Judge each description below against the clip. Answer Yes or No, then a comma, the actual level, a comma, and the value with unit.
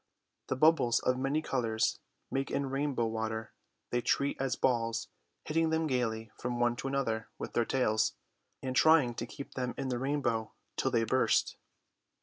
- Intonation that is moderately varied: Yes, average, 3.1 semitones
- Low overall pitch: Yes, low, 125 Hz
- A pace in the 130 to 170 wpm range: Yes, average, 165 wpm